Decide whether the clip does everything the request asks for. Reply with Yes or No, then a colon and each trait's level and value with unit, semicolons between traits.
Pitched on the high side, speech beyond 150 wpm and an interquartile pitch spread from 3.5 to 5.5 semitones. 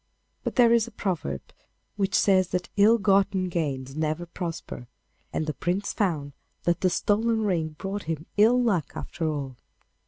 No: medium, 180 Hz; average, 160 wpm; average, 4.6 semitones